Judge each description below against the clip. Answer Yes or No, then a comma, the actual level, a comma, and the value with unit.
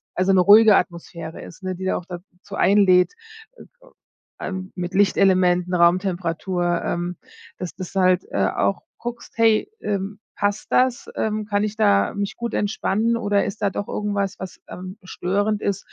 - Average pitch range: No, narrow, 2.3 semitones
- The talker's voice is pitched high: Yes, high, 195 Hz